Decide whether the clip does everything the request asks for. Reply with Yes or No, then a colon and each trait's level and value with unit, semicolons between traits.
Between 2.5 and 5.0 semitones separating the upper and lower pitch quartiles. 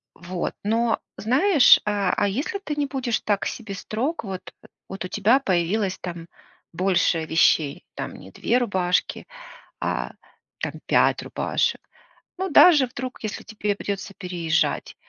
No: wide, 5.4 semitones